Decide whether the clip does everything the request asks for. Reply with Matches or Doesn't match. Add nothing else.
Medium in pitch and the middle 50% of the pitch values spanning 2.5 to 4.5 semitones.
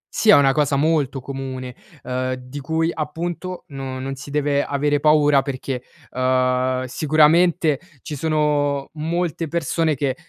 Matches